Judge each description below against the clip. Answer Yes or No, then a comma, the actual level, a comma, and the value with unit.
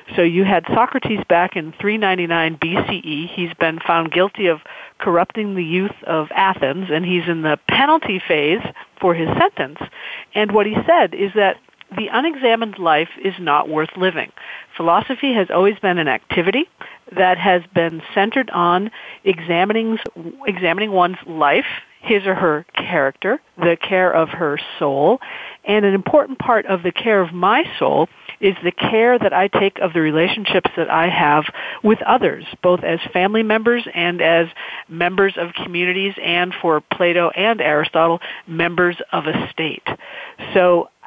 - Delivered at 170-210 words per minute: No, average, 155 wpm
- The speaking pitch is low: No, medium, 180 Hz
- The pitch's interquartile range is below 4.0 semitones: Yes, average, 3.3 semitones